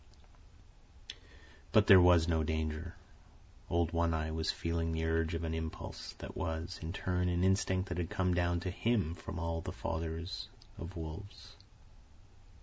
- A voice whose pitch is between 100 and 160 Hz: No, very low, 85 Hz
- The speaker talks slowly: No, average, 155 wpm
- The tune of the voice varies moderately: No, narrow, 1.8 semitones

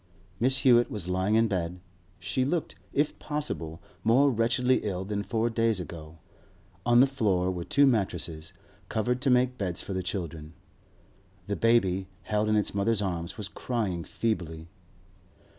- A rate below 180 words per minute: Yes, average, 155 wpm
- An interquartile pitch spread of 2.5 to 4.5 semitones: No, average, 5.1 semitones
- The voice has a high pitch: No, low, 105 Hz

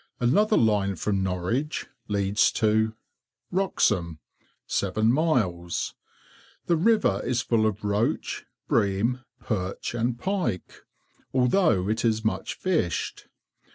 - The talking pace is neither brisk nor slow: No, slow, 105 wpm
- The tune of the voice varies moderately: Yes, average, 4.5 semitones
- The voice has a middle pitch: No, low, 110 Hz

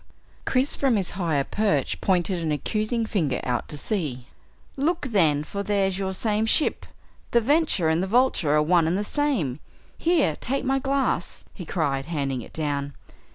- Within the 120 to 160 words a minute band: No, average, 170 wpm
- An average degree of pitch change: No, wide, 7.8 semitones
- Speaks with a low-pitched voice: No, high, 190 Hz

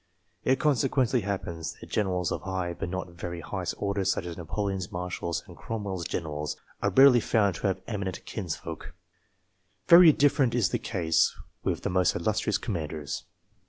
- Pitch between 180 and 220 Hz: No, very low, 95 Hz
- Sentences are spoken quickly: No, average, 165 wpm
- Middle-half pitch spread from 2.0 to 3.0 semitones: No, average, 4.3 semitones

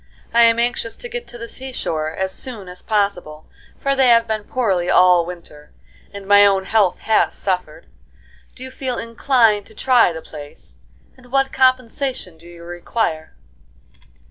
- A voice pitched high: Yes, high, 215 Hz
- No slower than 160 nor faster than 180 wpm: Yes, average, 170 wpm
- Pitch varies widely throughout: Yes, wide, 5.8 semitones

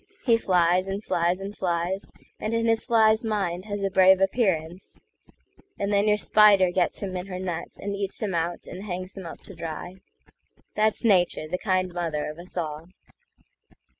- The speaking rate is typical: Yes, average, 165 wpm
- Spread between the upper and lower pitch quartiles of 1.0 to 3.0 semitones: Yes, average, 2.7 semitones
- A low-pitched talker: No, high, 190 Hz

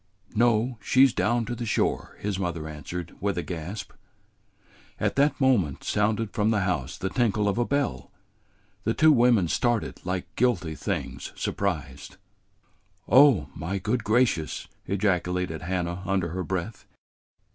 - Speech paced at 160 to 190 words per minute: No, average, 145 wpm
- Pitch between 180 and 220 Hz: No, low, 100 Hz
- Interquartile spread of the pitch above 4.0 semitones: Yes, average, 4.9 semitones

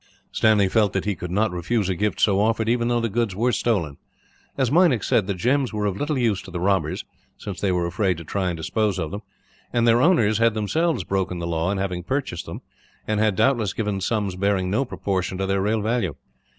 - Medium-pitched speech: No, low, 105 Hz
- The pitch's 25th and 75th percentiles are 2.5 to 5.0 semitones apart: Yes, average, 3.7 semitones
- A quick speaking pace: Yes, fast, 230 wpm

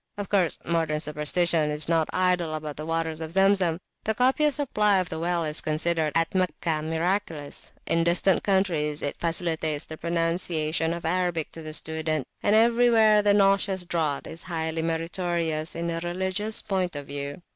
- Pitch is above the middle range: No, medium, 165 Hz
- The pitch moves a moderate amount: Yes, average, 3.0 semitones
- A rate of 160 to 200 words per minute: Yes, average, 165 wpm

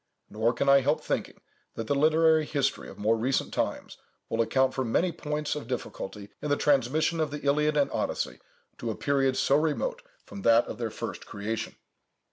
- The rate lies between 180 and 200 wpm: Yes, average, 190 wpm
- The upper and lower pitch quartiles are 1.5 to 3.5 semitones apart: No, average, 4.5 semitones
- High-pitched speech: No, medium, 140 Hz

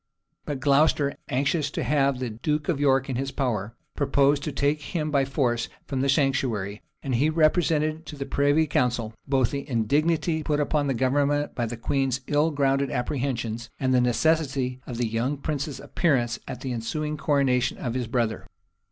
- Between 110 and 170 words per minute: No, average, 180 wpm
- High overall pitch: No, low, 135 Hz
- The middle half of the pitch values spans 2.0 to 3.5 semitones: Yes, average, 3.0 semitones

